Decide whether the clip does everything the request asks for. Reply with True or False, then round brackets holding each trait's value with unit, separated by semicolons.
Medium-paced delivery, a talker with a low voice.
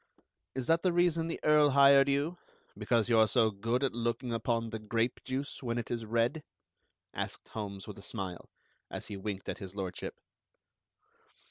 True (175 wpm; 115 Hz)